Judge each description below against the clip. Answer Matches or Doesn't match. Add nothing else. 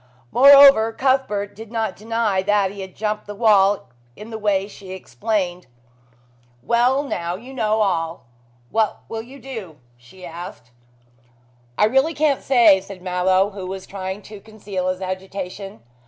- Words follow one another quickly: Doesn't match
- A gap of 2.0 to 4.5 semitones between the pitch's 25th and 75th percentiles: Matches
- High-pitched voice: Matches